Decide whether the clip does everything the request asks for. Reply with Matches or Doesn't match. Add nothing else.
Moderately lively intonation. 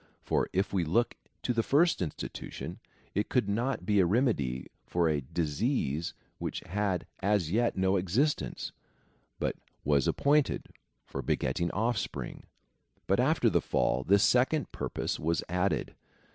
Doesn't match